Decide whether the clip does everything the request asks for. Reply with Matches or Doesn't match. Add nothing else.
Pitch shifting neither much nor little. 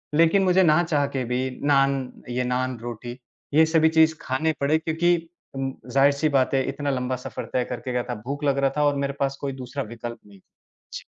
Matches